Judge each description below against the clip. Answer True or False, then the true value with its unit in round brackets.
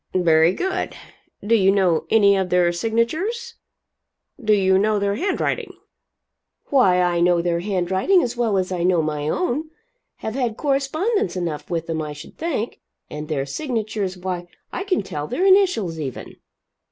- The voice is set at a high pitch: True (195 Hz)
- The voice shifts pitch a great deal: True (6.7 semitones)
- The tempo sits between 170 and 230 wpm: False (160 wpm)